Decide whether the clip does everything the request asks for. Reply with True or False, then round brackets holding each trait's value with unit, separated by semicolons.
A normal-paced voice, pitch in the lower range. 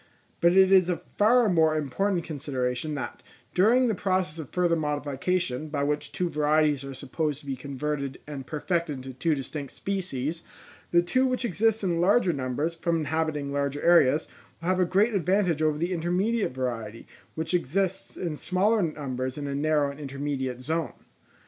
False (170 wpm; 155 Hz)